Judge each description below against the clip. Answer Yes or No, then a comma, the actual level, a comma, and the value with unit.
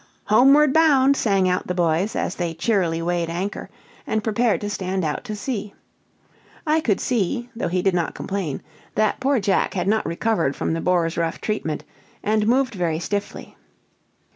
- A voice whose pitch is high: Yes, high, 200 Hz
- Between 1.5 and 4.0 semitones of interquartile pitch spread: No, average, 4.7 semitones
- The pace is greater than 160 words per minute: Yes, average, 170 wpm